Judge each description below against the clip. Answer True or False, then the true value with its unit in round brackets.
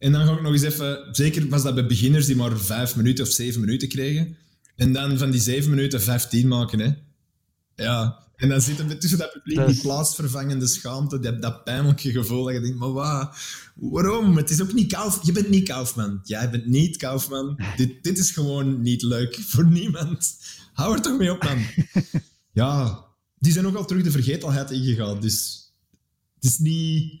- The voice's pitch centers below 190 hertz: True (135 Hz)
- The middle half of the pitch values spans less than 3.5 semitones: False (4.0 semitones)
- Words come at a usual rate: False (205 wpm)